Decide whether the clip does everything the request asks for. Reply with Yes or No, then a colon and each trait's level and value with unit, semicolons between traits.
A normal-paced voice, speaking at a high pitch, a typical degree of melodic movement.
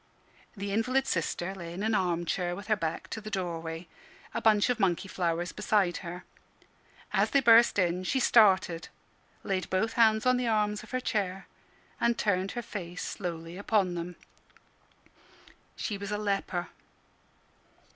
Yes: average, 155 wpm; high, 195 Hz; average, 3.7 semitones